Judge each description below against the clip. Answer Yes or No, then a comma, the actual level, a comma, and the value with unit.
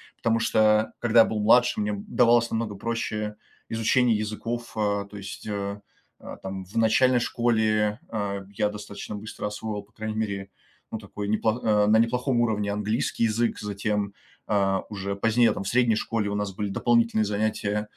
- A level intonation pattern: Yes, narrow, 1.9 semitones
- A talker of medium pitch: No, low, 105 Hz